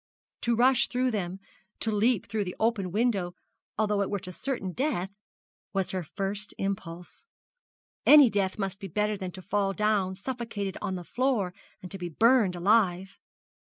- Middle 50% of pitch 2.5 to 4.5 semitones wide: Yes, average, 3.2 semitones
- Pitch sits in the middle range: No, high, 200 Hz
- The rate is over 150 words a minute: Yes, average, 165 wpm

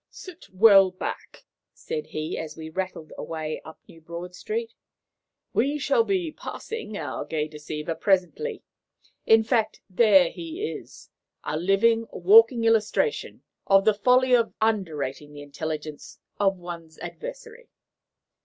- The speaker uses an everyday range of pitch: No, wide, 7.6 semitones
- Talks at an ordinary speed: No, slow, 130 wpm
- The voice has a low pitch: No, high, 195 Hz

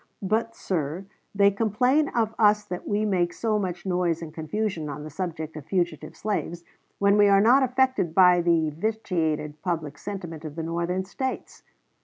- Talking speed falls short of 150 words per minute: No, average, 170 wpm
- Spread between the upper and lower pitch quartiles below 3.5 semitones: No, average, 4.5 semitones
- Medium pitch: Yes, medium, 180 Hz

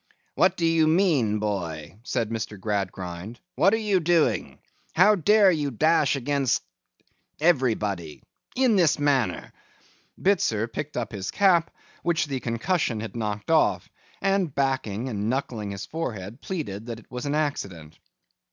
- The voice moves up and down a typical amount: No, wide, 7.6 semitones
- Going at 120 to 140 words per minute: Yes, slow, 135 wpm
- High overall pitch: No, low, 130 Hz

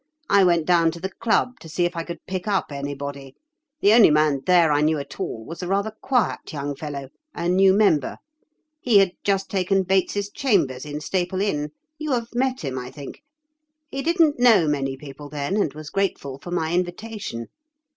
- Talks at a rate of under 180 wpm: No, average, 190 wpm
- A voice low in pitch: No, medium, 175 Hz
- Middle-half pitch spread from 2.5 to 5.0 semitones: No, wide, 5.5 semitones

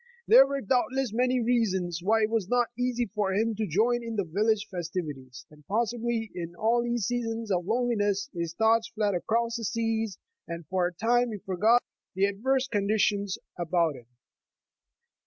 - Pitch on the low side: No, high, 215 Hz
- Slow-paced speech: No, average, 170 wpm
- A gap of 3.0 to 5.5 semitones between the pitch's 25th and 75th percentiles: Yes, average, 4.1 semitones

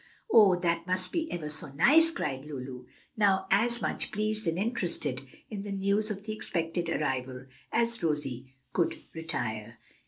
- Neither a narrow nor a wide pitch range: No, wide, 6.7 semitones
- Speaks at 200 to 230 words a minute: No, average, 155 wpm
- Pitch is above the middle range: No, medium, 175 Hz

